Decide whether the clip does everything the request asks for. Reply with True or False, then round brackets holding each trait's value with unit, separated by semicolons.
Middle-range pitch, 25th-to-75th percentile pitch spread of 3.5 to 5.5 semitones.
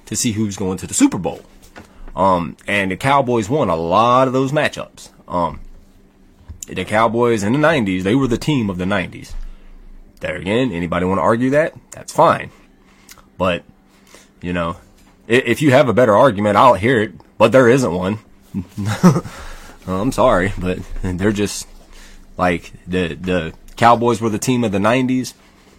False (100 Hz; 4.6 semitones)